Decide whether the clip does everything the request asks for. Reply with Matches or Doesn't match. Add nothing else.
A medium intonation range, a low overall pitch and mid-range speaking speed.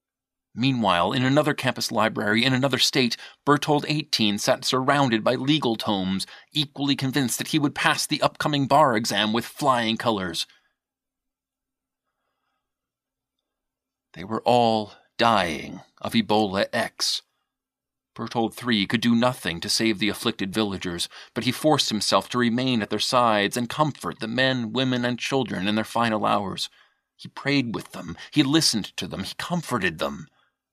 Matches